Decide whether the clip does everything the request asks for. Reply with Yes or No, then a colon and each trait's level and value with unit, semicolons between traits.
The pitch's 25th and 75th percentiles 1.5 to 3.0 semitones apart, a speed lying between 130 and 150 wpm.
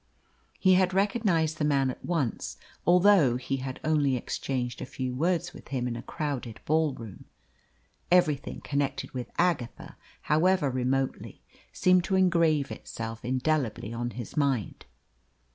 No: wide, 5.4 semitones; average, 140 wpm